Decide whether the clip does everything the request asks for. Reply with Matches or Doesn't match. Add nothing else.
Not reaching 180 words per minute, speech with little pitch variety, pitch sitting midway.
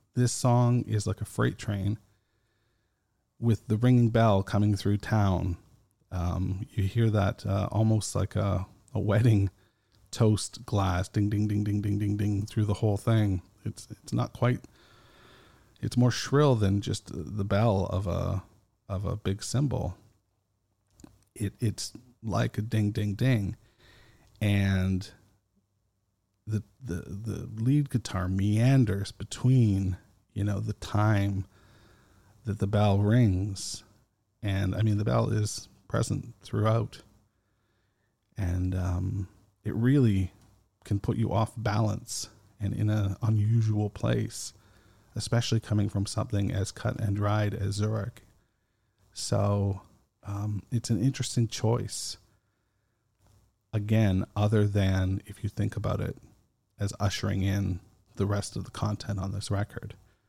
Doesn't match